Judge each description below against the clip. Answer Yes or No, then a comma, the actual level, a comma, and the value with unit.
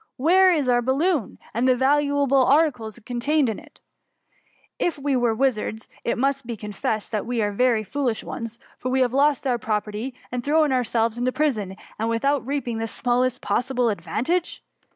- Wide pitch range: No, average, 3.6 semitones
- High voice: Yes, very high, 250 Hz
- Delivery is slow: No, average, 170 wpm